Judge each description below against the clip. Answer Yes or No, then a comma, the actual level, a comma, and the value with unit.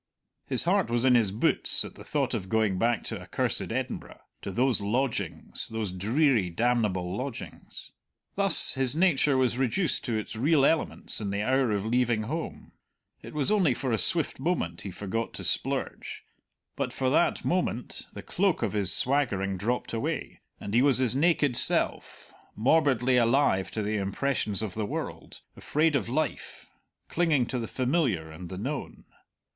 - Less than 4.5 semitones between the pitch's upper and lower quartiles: No, average, 4.9 semitones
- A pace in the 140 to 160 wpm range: No, average, 170 wpm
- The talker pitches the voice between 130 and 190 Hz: No, low, 120 Hz